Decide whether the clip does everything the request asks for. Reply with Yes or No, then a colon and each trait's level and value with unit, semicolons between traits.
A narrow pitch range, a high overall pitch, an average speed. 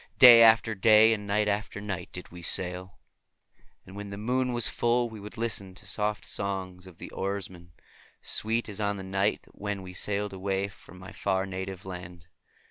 No: narrow, 2.3 semitones; low, 100 Hz; average, 190 wpm